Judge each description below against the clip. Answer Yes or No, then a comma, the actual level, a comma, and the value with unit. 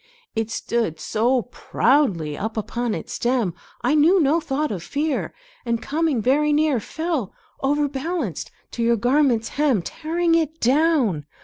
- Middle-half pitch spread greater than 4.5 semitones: Yes, average, 5.2 semitones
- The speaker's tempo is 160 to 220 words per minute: No, average, 140 wpm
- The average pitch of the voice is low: No, very high, 265 Hz